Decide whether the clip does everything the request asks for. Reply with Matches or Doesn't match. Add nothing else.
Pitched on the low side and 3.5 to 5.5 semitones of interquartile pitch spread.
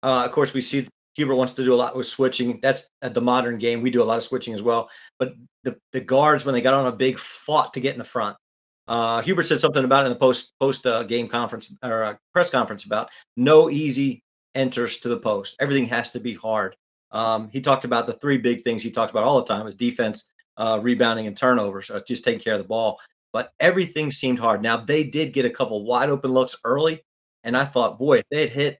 Doesn't match